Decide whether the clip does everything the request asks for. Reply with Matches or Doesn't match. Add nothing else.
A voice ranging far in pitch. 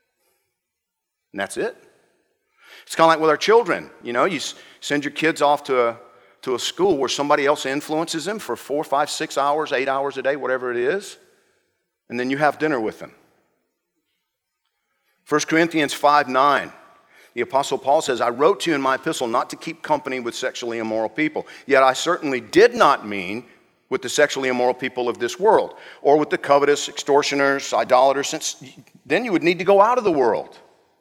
Doesn't match